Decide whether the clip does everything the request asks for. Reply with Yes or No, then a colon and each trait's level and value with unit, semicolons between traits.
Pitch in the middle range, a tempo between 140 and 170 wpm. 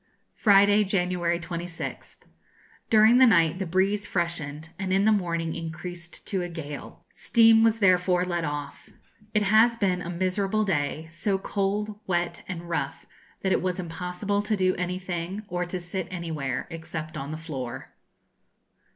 Yes: medium, 180 Hz; average, 150 wpm